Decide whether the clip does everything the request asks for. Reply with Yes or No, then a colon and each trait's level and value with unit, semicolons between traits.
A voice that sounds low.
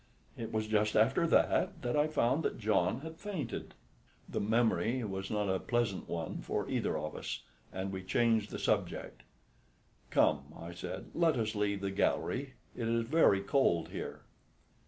Yes: low, 110 Hz